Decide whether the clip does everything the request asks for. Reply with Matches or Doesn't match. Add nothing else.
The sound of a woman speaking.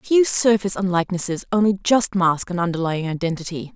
Matches